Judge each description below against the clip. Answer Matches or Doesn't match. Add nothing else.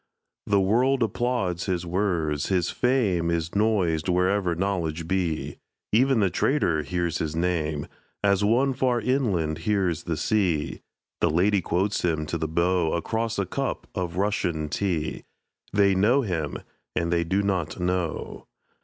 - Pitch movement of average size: Matches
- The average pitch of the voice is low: Matches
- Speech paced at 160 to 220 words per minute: Doesn't match